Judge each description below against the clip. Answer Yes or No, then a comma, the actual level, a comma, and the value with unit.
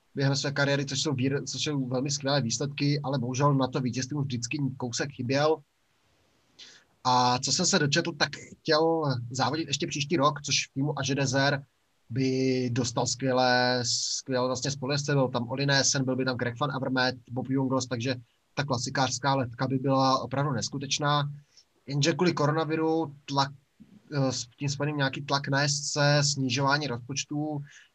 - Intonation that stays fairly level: Yes, narrow, 2.0 semitones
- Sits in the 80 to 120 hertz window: No, medium, 140 Hz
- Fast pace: No, average, 155 wpm